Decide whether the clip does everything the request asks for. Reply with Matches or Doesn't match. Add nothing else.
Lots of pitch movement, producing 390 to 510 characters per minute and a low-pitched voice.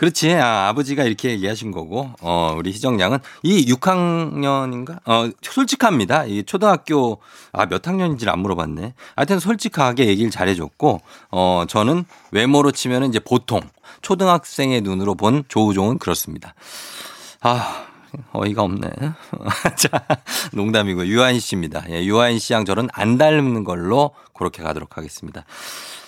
Doesn't match